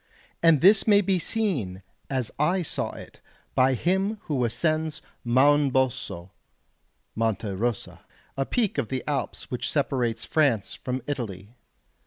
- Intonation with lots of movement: Yes, wide, 5.7 semitones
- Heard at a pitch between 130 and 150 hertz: Yes, low, 135 Hz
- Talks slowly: Yes, slow, 130 wpm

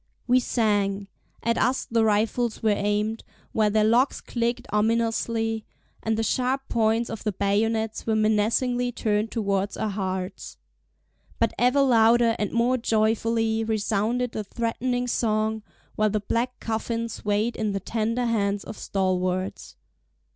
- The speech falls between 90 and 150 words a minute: Yes, average, 140 wpm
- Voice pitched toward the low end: No, high, 220 Hz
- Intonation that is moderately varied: No, narrow, 1.9 semitones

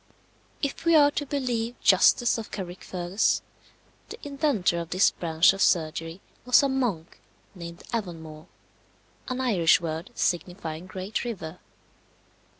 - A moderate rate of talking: No, slow, 125 wpm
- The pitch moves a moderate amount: No, wide, 6.4 semitones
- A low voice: No, high, 190 Hz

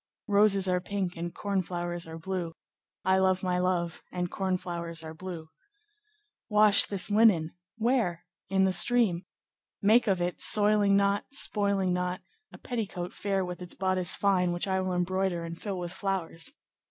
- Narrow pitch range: Yes, narrow, 2.2 semitones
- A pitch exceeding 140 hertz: Yes, medium, 185 Hz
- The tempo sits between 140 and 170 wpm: Yes, average, 155 wpm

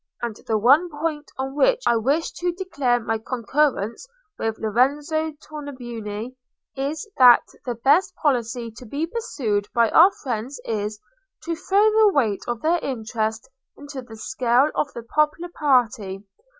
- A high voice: Yes, very high, 260 Hz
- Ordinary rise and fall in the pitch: Yes, average, 5.0 semitones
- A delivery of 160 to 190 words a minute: No, average, 150 wpm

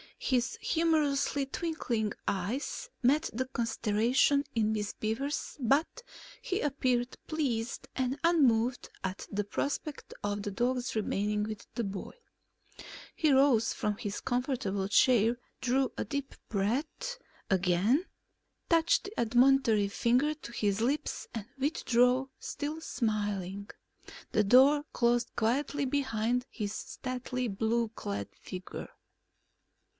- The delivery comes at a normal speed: No, slow, 115 wpm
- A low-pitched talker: No, high, 245 Hz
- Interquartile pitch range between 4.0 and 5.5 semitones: Yes, average, 4.6 semitones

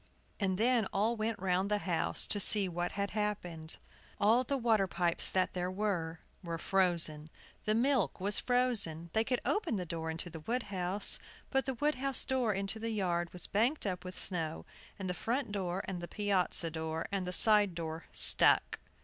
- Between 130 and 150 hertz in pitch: No, high, 195 Hz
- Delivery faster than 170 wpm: Yes, average, 190 wpm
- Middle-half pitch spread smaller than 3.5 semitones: No, average, 4.1 semitones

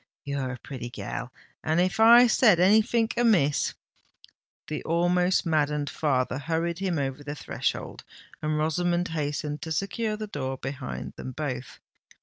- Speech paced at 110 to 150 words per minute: Yes, slow, 135 wpm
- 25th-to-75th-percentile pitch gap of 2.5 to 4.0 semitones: No, average, 4.5 semitones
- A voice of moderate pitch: Yes, medium, 155 Hz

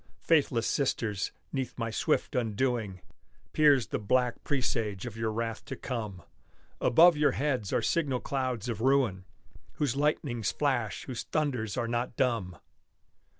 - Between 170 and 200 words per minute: No, average, 140 wpm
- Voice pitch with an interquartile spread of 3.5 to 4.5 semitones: Yes, average, 3.8 semitones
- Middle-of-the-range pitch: No, low, 120 Hz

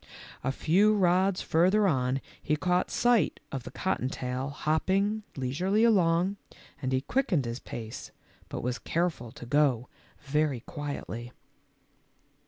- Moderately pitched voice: Yes, medium, 150 Hz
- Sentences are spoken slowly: Yes, slow, 130 wpm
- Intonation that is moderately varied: No, wide, 6.5 semitones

